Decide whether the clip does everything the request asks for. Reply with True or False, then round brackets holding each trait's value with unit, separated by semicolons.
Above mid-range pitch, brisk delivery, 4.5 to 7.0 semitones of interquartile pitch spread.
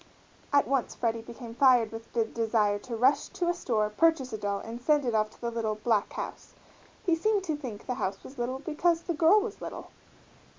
True (245 Hz; 215 wpm; 5.2 semitones)